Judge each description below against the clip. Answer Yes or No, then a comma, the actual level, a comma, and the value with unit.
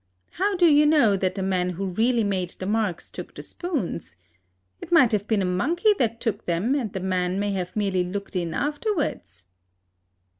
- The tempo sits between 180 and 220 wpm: Yes, average, 190 wpm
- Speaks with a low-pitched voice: No, high, 205 Hz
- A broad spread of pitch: Yes, wide, 7.1 semitones